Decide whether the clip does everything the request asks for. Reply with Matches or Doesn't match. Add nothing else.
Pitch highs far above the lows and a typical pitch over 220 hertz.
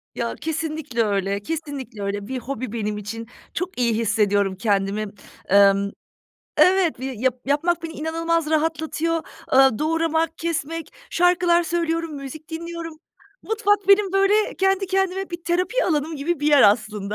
Matches